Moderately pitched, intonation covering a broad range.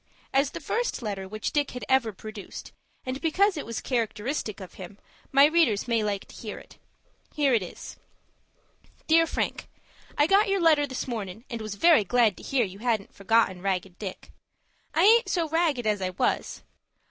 No: high, 235 Hz; wide, 6.5 semitones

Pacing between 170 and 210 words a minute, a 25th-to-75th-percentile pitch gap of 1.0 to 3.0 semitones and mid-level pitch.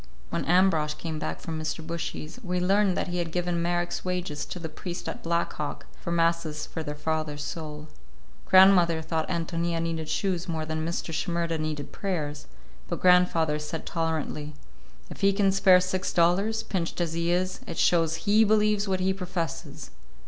Yes: average, 175 wpm; narrow, 2.4 semitones; medium, 170 Hz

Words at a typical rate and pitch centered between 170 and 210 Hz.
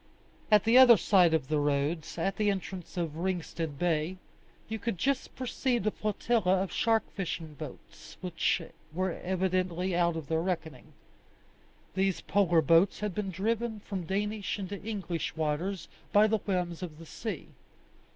Yes: average, 155 wpm; medium, 185 Hz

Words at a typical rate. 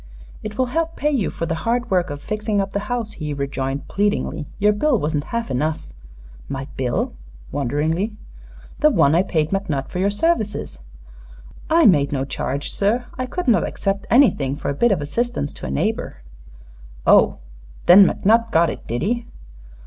Yes: average, 175 wpm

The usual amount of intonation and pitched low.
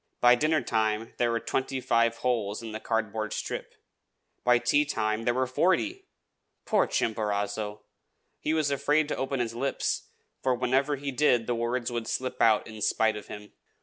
Yes: average, 3.4 semitones; low, 120 Hz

